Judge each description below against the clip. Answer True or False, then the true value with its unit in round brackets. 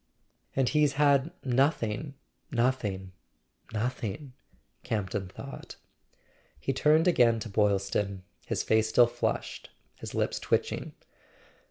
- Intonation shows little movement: False (4.9 semitones)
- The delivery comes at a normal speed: False (105 wpm)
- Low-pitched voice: True (120 Hz)